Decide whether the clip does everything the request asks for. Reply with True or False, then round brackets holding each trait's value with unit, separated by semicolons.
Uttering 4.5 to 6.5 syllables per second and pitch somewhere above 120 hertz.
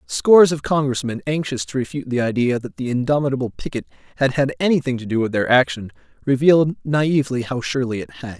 True (6.3 syllables/s; 135 Hz)